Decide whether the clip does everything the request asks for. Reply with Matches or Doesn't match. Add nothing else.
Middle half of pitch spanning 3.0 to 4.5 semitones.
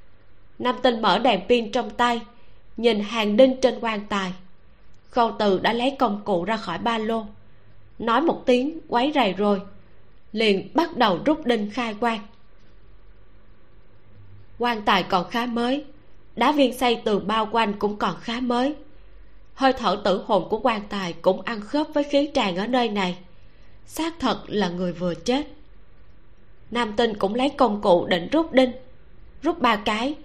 Doesn't match